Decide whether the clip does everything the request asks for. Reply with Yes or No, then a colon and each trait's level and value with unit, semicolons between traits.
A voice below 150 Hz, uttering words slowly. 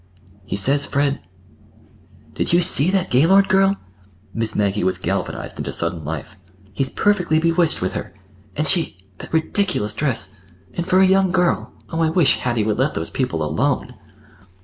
No: medium, 140 Hz; average, 155 wpm